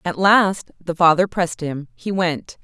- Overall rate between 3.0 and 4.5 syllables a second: Yes, 4.2 syllables/s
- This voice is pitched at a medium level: Yes, medium, 175 Hz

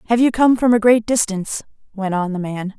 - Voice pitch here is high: Yes, high, 215 Hz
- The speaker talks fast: Yes, fast, 235 wpm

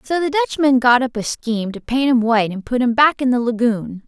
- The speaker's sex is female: Yes, female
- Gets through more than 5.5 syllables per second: Yes, 5.8 syllables/s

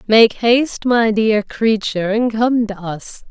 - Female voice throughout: Yes, female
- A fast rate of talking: No, average, 165 wpm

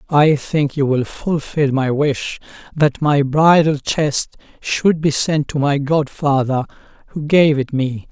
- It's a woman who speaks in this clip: No, male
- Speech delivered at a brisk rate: No, average, 155 wpm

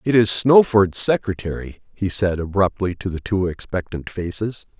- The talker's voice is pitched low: Yes, low, 100 Hz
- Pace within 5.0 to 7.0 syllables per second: No, 4.7 syllables/s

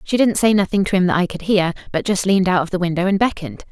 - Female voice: Yes, female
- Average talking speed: No, fast, 305 wpm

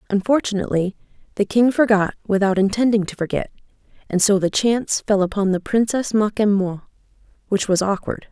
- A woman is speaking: Yes, female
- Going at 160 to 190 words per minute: No, average, 145 wpm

